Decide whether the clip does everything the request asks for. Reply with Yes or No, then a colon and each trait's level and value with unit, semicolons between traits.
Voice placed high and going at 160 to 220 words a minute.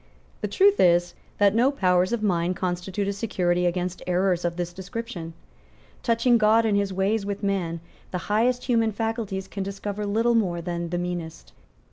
Yes: high, 195 Hz; average, 170 wpm